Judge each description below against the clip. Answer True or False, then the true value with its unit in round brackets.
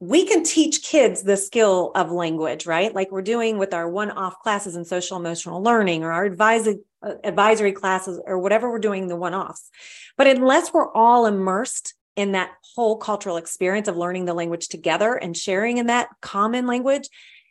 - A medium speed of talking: True (180 wpm)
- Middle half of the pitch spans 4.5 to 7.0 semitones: False (4.1 semitones)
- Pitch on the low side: False (200 Hz)